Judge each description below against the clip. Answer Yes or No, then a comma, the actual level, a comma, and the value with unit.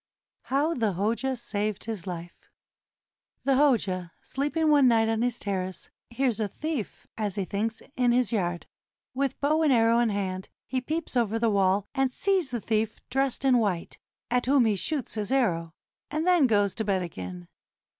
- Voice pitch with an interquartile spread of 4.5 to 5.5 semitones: Yes, average, 5.1 semitones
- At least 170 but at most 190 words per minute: Yes, average, 175 wpm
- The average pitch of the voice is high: Yes, high, 230 Hz